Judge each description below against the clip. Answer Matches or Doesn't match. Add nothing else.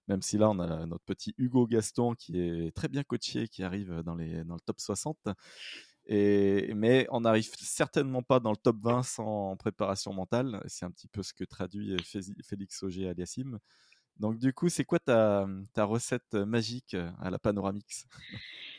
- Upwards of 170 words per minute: Matches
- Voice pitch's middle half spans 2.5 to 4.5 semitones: Matches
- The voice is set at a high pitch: Doesn't match